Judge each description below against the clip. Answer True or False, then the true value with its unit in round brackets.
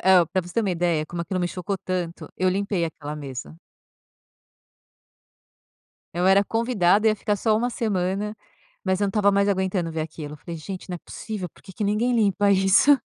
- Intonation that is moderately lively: True (3.0 semitones)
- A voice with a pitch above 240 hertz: False (190 Hz)